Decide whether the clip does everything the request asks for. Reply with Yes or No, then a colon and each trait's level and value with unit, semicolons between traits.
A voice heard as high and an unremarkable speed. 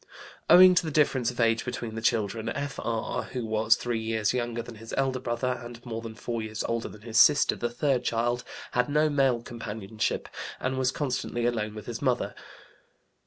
No: low, 120 Hz; average, 190 wpm